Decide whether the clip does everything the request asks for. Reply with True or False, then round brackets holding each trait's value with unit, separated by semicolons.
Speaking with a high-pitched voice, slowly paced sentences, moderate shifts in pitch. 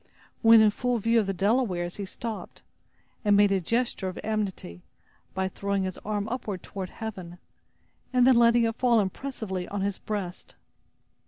False (205 Hz; 165 wpm; 3.4 semitones)